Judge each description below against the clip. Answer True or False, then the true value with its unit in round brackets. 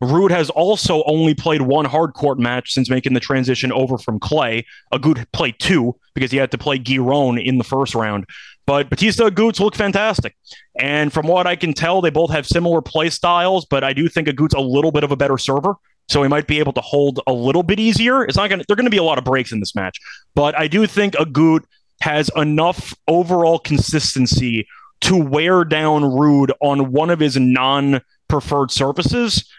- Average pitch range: True (4.0 semitones)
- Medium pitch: True (150 Hz)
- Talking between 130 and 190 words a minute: False (205 wpm)